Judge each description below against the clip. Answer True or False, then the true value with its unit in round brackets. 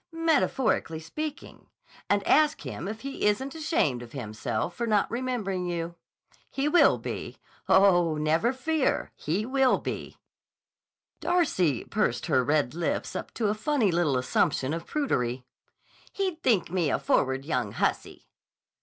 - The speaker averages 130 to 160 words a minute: True (140 wpm)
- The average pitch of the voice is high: True (195 Hz)